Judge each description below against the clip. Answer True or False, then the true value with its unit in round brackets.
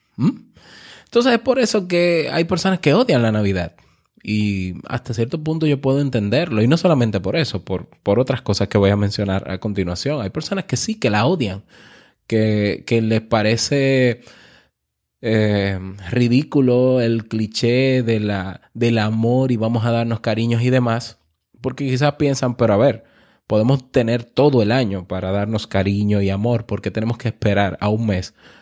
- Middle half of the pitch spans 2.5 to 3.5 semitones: False (3.9 semitones)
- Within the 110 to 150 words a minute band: False (175 wpm)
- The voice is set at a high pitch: False (115 Hz)